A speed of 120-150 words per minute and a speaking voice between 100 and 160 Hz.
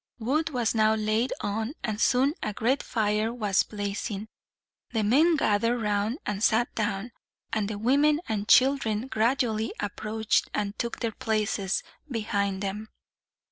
No: average, 140 wpm; high, 220 Hz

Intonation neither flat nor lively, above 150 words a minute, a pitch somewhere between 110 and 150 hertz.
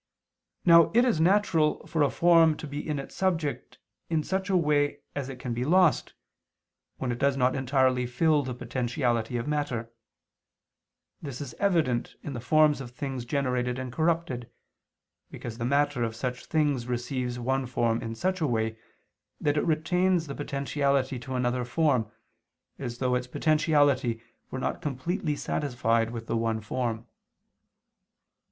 Yes: average, 4.0 semitones; average, 160 wpm; low, 135 Hz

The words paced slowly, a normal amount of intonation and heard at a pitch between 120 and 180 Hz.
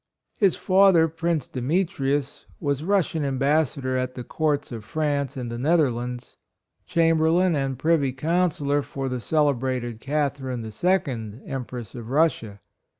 Yes: slow, 130 wpm; average, 4.0 semitones; medium, 140 Hz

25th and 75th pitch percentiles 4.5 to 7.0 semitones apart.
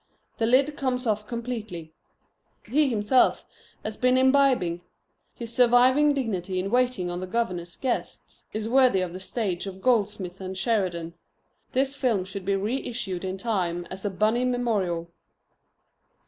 Yes: average, 5.1 semitones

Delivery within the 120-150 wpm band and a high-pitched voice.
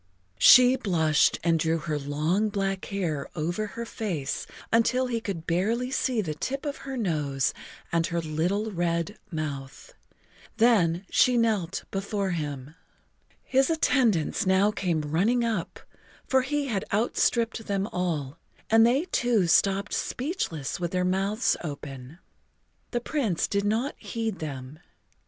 Yes: average, 140 wpm; high, 195 Hz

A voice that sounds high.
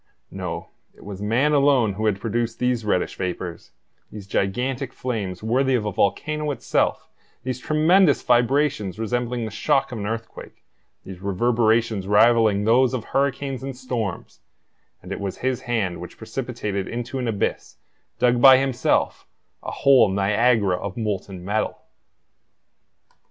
No: low, 115 Hz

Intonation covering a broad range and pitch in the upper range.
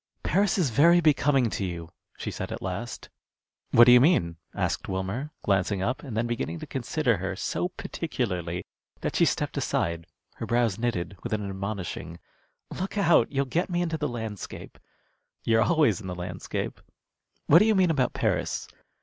No: wide, 8.0 semitones; low, 115 Hz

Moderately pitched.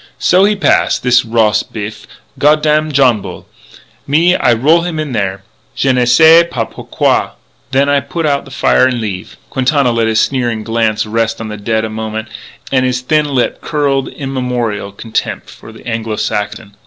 No: low, 120 Hz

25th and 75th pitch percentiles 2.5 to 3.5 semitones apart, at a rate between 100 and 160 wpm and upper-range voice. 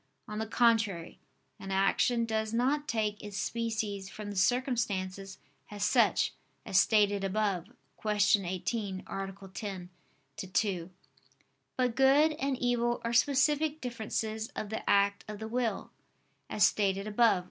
Yes: average, 3.2 semitones; average, 140 wpm; high, 215 Hz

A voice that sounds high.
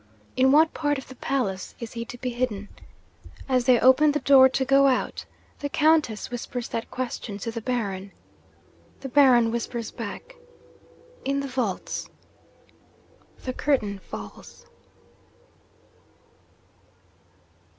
Yes: very high, 250 Hz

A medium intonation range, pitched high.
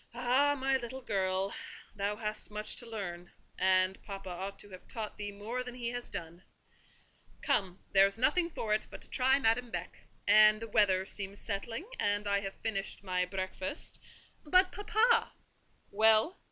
Yes: average, 4.0 semitones; high, 210 Hz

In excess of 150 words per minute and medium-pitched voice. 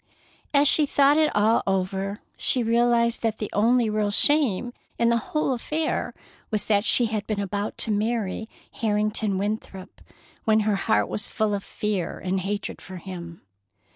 No: average, 165 wpm; high, 215 Hz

